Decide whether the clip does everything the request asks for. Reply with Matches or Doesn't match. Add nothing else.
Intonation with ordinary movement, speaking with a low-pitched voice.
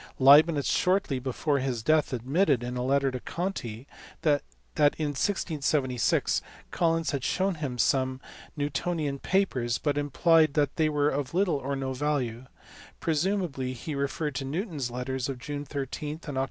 Doesn't match